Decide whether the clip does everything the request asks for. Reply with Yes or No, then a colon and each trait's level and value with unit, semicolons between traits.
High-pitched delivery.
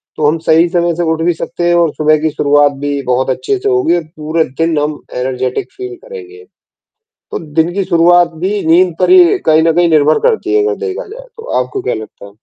No: medium, 170 Hz